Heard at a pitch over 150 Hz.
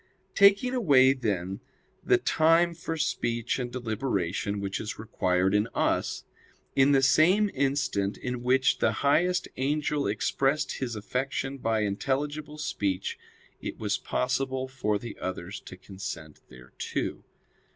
No: low, 130 Hz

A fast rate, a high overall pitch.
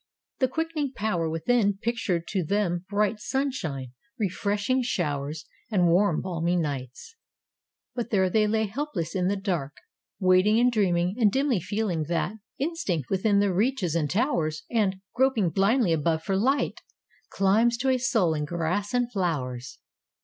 No: average, 150 wpm; high, 195 Hz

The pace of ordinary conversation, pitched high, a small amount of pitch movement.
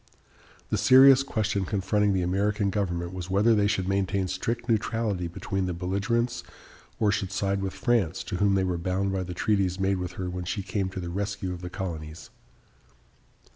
No: average, 185 wpm; very low, 95 Hz; narrow, 2.1 semitones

